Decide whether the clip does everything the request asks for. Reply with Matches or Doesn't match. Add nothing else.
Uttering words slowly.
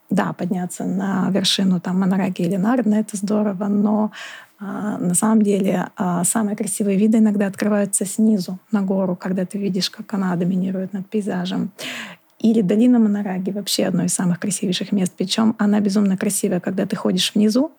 Doesn't match